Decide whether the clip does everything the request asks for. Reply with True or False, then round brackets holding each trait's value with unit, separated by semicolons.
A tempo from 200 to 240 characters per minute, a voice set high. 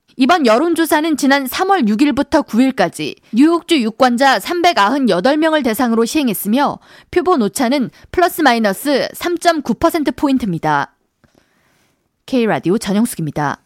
False (270 characters per minute; 270 Hz)